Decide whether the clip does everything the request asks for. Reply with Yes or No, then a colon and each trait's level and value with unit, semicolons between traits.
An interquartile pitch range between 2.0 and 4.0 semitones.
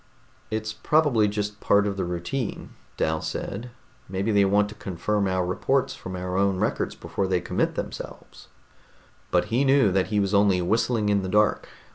Yes: narrow, 2.5 semitones